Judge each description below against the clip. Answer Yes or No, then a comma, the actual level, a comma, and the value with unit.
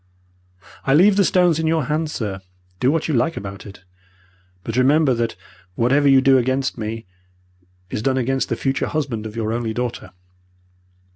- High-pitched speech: No, low, 130 Hz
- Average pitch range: Yes, average, 4.8 semitones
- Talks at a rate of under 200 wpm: Yes, average, 170 wpm